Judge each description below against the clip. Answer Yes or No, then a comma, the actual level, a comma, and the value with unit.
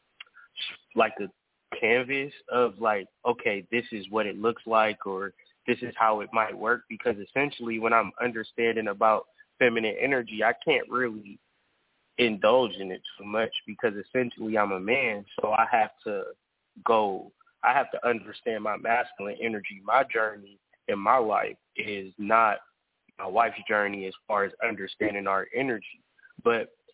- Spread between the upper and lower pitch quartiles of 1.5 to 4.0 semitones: Yes, average, 3.1 semitones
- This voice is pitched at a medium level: No, low, 110 Hz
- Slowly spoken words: No, average, 155 wpm